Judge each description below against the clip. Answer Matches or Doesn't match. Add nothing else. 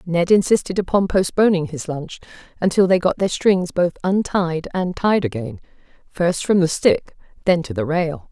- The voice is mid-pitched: Matches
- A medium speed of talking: Matches